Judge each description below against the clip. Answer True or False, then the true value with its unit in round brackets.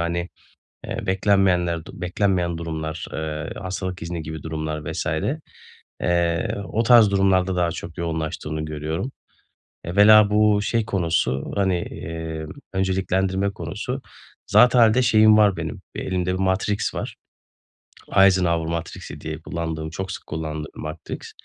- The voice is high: False (90 Hz)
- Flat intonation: False (3.3 semitones)